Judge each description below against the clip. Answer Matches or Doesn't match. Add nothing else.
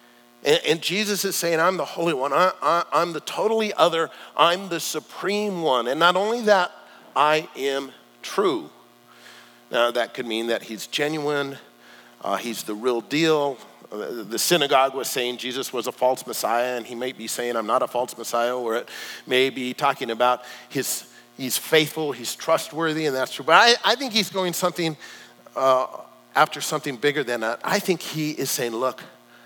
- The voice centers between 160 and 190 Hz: Doesn't match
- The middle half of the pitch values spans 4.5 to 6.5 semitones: Matches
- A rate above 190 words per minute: Doesn't match